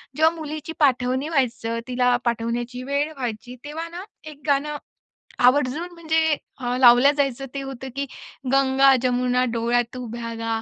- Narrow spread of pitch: No, average, 3.0 semitones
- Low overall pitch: No, very high, 260 Hz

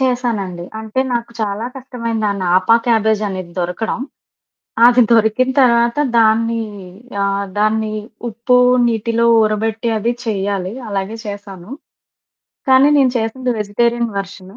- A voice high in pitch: Yes, high, 220 Hz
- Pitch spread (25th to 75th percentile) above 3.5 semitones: No, average, 2.8 semitones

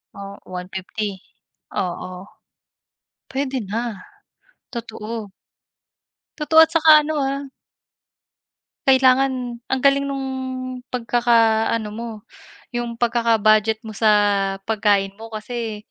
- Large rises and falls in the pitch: No, average, 3.7 semitones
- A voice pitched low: No, high, 230 Hz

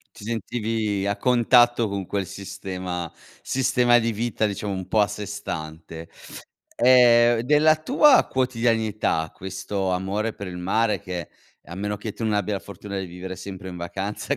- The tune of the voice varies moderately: Yes, average, 3.7 semitones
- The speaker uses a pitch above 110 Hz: No, low, 105 Hz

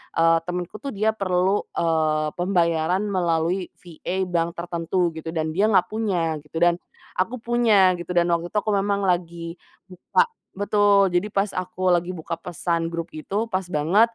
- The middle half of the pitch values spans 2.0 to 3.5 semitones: Yes, average, 2.9 semitones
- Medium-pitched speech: Yes, medium, 180 Hz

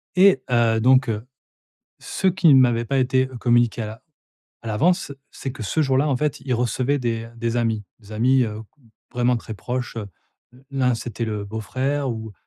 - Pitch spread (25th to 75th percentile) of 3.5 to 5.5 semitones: No, average, 2.8 semitones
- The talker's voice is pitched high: No, low, 120 Hz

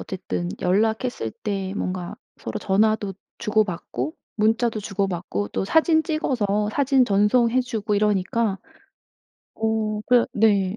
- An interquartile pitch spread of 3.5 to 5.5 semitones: No, average, 3.0 semitones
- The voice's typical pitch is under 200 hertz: No, high, 210 Hz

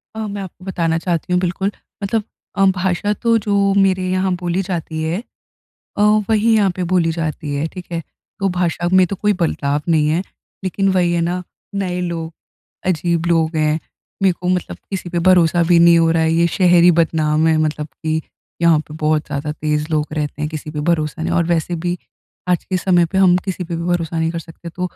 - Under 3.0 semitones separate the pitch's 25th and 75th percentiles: Yes, narrow, 2.5 semitones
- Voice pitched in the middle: Yes, medium, 170 Hz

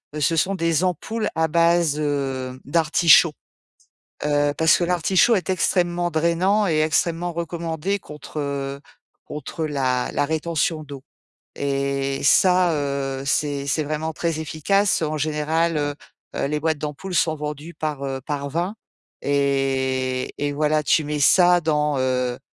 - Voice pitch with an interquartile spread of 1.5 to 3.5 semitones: Yes, average, 3.1 semitones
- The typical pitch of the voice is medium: Yes, medium, 150 Hz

